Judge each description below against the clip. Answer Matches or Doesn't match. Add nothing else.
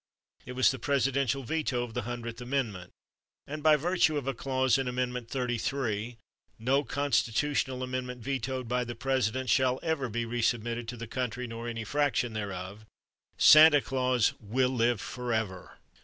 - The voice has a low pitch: Matches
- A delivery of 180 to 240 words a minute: Doesn't match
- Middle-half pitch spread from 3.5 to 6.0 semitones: Doesn't match